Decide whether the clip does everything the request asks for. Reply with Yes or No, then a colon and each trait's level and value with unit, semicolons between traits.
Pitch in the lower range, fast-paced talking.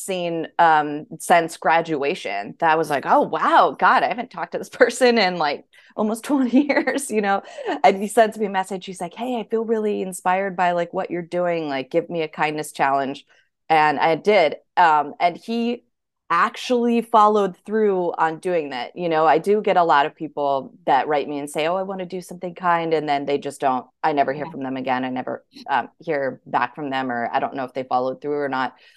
No: medium, 170 Hz; fast, 225 wpm